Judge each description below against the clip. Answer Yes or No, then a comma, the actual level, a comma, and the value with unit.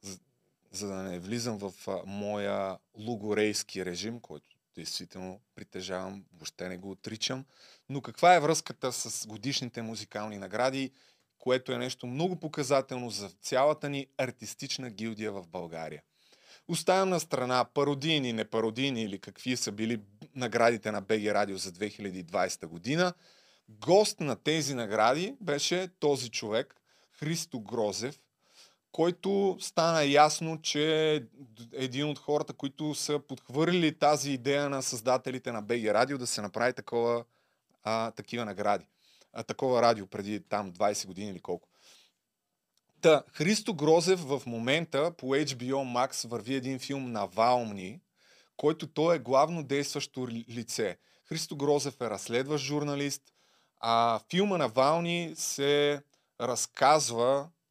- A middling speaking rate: Yes, average, 130 wpm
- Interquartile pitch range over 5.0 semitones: Yes, wide, 5.5 semitones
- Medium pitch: No, low, 130 Hz